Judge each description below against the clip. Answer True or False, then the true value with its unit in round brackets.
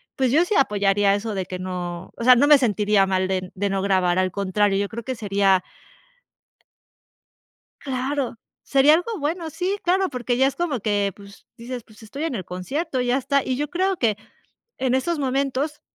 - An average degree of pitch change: False (6.0 semitones)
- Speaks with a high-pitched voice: True (245 Hz)